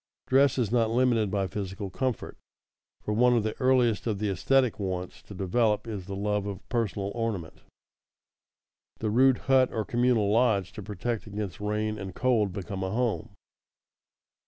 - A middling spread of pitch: Yes, average, 3.4 semitones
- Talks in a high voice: No, low, 105 Hz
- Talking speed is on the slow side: No, average, 160 wpm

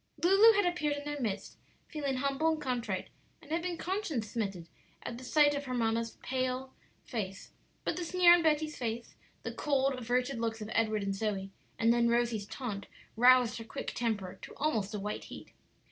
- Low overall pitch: No, very high, 250 Hz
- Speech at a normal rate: Yes, average, 185 wpm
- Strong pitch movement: No, average, 5.0 semitones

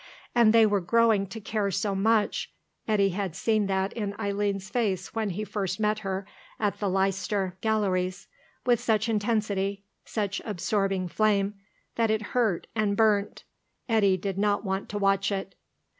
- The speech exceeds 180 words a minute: No, average, 160 wpm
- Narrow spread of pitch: Yes, narrow, 1.8 semitones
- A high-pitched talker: Yes, high, 205 Hz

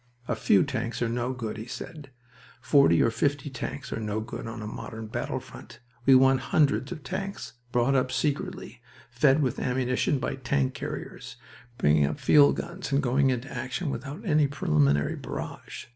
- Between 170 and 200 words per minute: Yes, average, 175 wpm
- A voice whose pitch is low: Yes, low, 130 Hz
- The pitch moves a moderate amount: Yes, average, 3.4 semitones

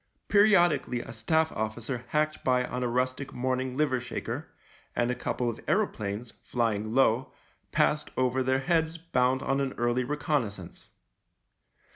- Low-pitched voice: Yes, low, 130 Hz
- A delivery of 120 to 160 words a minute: Yes, average, 150 wpm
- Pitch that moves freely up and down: No, average, 3.8 semitones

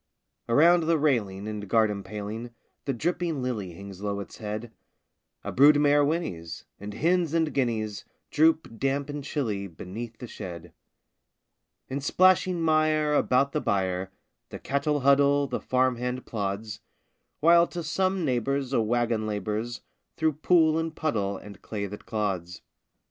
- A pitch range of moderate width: No, wide, 6.6 semitones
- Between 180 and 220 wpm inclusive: No, average, 145 wpm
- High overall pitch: No, low, 125 Hz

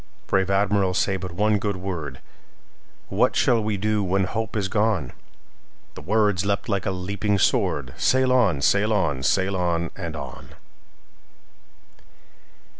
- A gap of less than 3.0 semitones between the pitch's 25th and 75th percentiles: Yes, narrow, 2.4 semitones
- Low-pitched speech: Yes, low, 100 Hz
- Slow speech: Yes, slow, 125 wpm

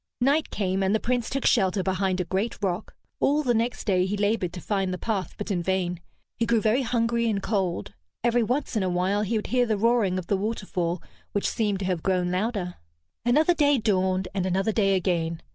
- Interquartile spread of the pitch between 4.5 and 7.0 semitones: No, average, 3.8 semitones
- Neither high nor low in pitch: No, high, 200 Hz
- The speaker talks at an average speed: No, fast, 215 wpm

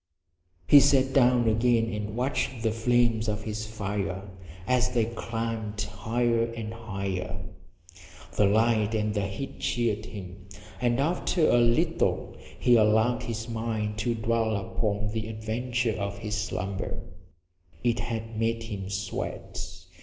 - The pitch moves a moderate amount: No, narrow, 2.2 semitones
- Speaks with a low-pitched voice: Yes, low, 110 Hz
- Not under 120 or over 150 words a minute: Yes, slow, 135 wpm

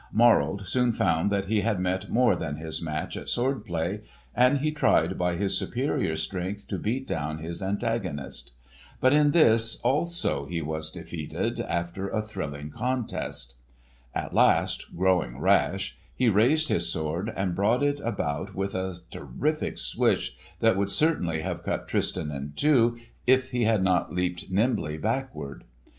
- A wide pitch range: Yes, wide, 6.4 semitones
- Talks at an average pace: Yes, average, 155 wpm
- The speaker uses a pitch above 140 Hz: No, very low, 95 Hz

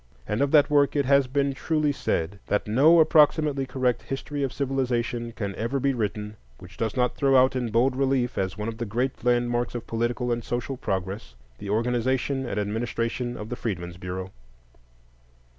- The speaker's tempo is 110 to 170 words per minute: No, average, 180 wpm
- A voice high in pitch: No, low, 120 Hz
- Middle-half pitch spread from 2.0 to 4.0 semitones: Yes, average, 3.6 semitones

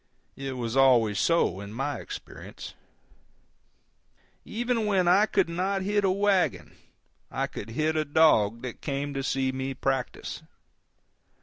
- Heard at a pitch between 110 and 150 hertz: Yes, medium, 140 Hz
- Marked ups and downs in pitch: Yes, wide, 6.8 semitones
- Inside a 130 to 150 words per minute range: Yes, slow, 135 wpm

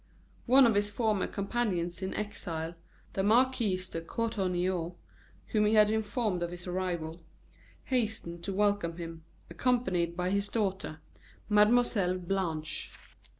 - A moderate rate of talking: No, slow, 125 wpm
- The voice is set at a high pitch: Yes, high, 195 Hz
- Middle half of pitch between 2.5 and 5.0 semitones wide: Yes, average, 3.8 semitones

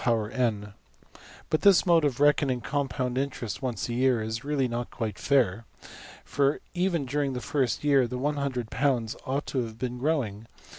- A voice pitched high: No, low, 130 Hz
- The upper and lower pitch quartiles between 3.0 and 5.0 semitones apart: Yes, average, 3.4 semitones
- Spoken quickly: No, average, 155 wpm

